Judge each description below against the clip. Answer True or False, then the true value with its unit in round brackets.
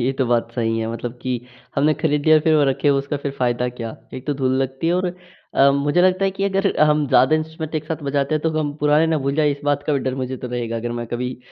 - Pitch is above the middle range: False (140 Hz)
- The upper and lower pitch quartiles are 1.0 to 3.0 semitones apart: False (3.5 semitones)